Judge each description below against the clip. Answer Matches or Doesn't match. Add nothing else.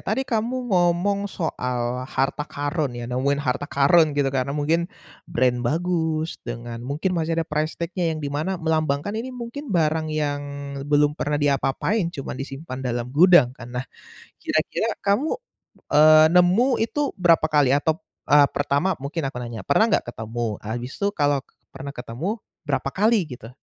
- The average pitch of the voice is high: Doesn't match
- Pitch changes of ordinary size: Matches